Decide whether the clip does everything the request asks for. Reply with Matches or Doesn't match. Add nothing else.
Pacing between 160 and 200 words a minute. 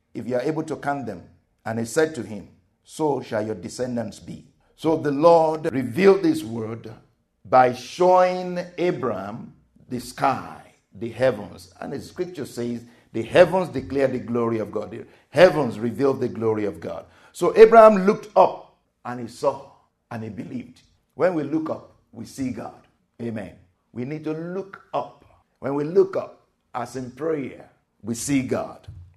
Matches